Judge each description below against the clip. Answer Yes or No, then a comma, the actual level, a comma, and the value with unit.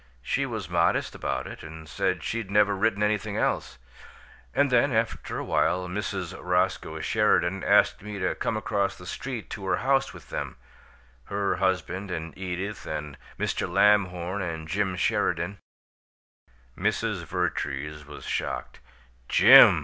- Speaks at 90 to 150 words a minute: Yes, average, 145 wpm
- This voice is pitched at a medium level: No, very low, 95 Hz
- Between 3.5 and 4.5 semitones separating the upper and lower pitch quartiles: No, average, 3.1 semitones